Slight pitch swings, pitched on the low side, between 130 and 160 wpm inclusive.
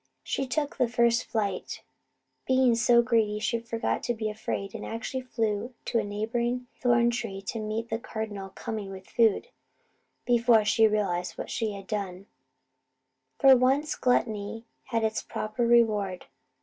No: narrow, 2.2 semitones; high, 225 Hz; average, 150 wpm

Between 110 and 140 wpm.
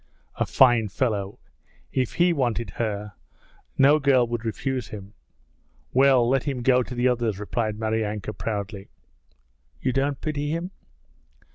Yes: slow, 135 wpm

